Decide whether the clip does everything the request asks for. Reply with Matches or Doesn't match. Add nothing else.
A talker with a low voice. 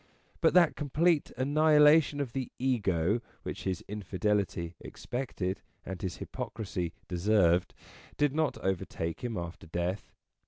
Matches